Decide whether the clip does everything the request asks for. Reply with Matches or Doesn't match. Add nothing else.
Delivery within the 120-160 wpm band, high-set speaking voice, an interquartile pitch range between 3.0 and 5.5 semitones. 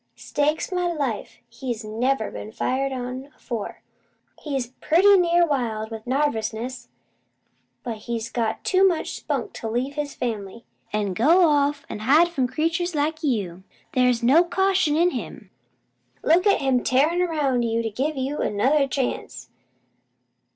Matches